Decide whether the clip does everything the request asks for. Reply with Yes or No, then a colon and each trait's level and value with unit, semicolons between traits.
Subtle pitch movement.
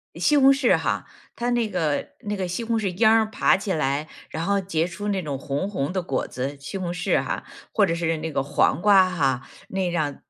No: average, 5.0 semitones